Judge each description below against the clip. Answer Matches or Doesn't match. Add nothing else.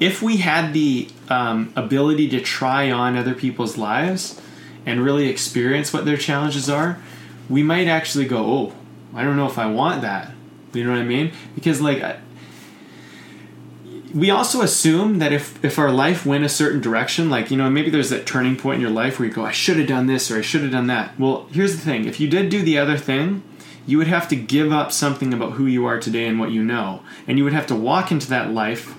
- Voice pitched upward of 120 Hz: Matches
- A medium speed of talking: Doesn't match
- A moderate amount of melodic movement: Matches